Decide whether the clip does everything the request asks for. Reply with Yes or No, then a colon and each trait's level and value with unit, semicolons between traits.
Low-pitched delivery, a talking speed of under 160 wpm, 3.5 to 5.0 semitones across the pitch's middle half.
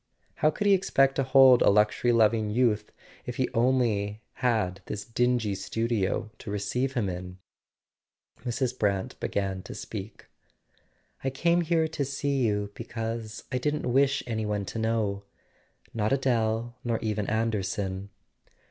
Yes: low, 115 Hz; average, 145 wpm; average, 3.8 semitones